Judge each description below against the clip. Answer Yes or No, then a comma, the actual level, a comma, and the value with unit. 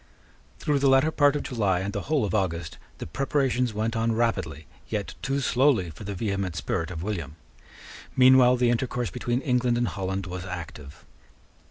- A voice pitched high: No, low, 110 Hz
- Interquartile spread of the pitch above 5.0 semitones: Yes, wide, 5.6 semitones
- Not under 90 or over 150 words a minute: No, average, 175 wpm